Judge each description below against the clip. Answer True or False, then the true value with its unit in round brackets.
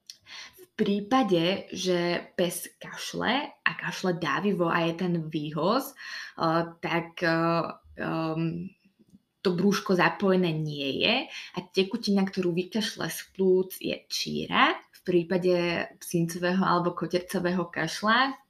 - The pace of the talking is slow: True (105 wpm)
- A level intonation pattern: True (2.3 semitones)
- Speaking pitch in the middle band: True (180 Hz)